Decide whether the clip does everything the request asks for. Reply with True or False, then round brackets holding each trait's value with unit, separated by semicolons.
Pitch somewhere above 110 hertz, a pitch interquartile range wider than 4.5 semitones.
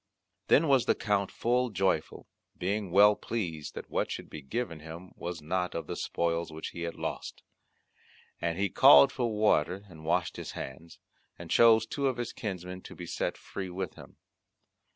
False (95 Hz; 5.0 semitones)